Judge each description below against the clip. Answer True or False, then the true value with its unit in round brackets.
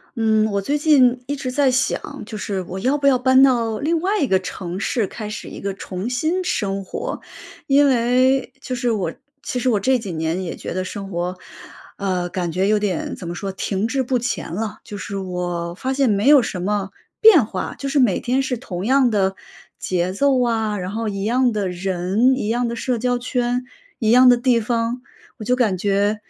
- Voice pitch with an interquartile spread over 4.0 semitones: True (4.8 semitones)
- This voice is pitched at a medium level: False (225 Hz)